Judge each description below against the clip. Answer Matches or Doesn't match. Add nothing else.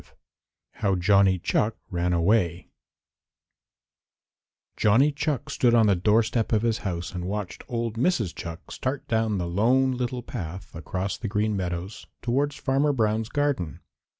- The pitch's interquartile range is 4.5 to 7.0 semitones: Matches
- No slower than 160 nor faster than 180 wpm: Doesn't match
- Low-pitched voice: Matches